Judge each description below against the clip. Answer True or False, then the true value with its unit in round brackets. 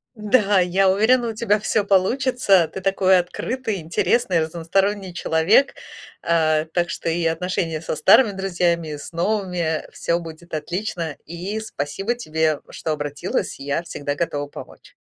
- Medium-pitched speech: True (175 Hz)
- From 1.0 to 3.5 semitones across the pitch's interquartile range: False (4.0 semitones)